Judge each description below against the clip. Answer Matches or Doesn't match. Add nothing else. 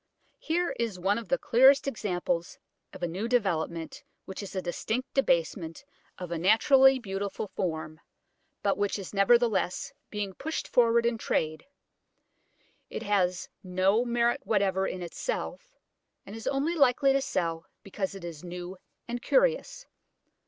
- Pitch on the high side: Matches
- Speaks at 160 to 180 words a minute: Doesn't match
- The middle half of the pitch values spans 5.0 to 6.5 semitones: Matches